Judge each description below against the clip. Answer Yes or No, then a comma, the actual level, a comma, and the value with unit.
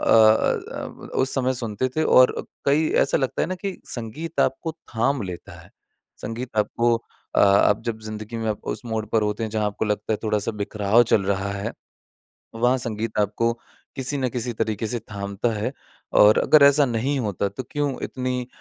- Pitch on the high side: No, low, 115 Hz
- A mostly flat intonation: No, average, 3.5 semitones